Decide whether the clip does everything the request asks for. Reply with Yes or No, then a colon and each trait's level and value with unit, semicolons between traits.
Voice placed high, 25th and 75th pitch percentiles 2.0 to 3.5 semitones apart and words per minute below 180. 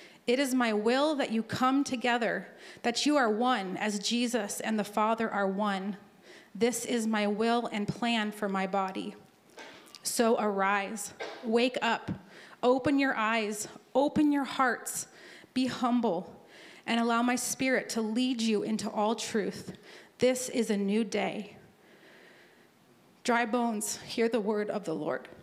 Yes: high, 230 Hz; average, 2.9 semitones; average, 150 wpm